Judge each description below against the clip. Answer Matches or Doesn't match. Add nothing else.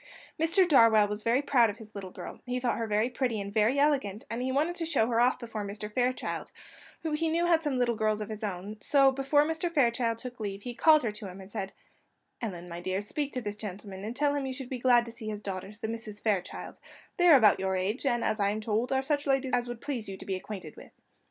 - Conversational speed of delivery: Doesn't match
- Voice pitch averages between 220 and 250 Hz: Matches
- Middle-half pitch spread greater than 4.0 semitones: Matches